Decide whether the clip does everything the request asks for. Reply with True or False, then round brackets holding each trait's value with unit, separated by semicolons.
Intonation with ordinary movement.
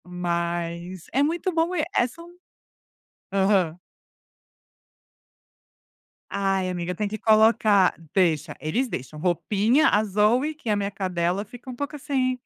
False (6.1 semitones)